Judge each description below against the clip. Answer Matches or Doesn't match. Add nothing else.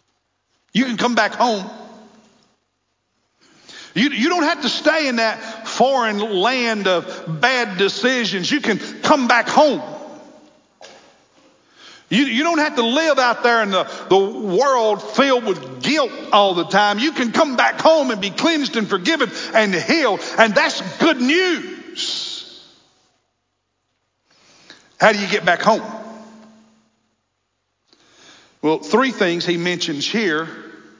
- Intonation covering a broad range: Matches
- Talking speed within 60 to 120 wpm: Doesn't match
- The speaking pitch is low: Doesn't match